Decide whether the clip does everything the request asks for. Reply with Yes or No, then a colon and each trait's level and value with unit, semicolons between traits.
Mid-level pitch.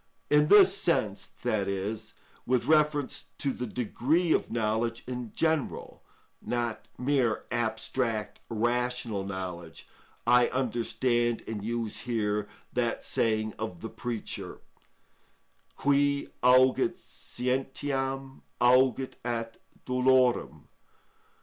No: low, 120 Hz